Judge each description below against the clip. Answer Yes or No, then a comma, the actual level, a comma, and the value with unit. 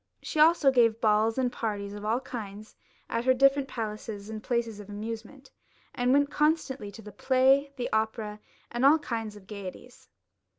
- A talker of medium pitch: No, high, 230 Hz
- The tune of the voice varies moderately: Yes, average, 3.9 semitones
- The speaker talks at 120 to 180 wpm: Yes, average, 170 wpm